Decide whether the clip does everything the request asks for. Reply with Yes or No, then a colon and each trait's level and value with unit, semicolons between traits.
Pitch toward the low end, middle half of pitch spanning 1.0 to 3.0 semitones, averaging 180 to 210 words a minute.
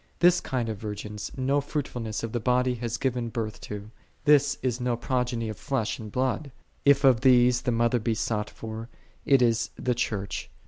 Yes: low, 120 Hz; narrow, 2.6 semitones; average, 185 wpm